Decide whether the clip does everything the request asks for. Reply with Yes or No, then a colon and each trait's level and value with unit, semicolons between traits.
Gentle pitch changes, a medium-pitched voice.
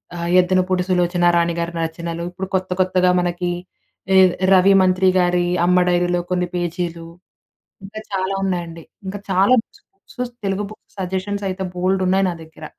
Yes: narrow, 1.3 semitones; medium, 180 Hz